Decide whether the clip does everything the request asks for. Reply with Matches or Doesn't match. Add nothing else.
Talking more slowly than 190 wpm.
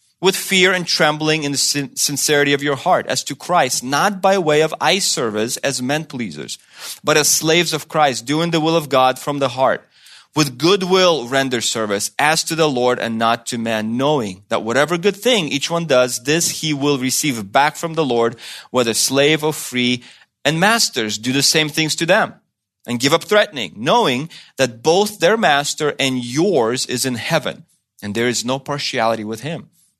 Doesn't match